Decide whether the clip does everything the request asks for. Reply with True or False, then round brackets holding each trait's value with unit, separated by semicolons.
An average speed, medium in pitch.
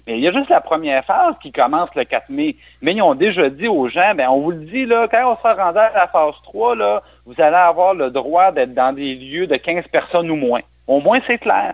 False (270 wpm; 180 Hz)